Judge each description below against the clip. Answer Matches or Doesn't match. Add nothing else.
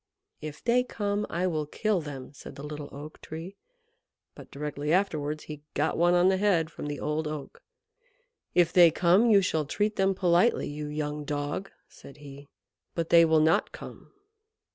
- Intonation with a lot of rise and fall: Doesn't match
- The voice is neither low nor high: Matches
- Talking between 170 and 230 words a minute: Matches